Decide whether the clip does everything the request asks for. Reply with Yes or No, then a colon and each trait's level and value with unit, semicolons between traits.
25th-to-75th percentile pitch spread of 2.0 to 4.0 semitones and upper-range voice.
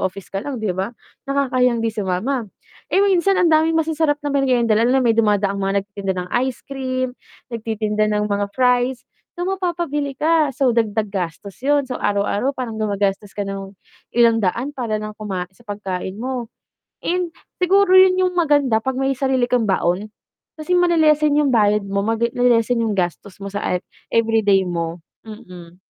No: wide, 5.6 semitones; high, 230 Hz